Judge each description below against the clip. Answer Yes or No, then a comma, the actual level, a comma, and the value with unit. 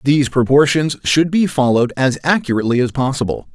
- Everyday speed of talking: Yes, average, 150 wpm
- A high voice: No, low, 135 Hz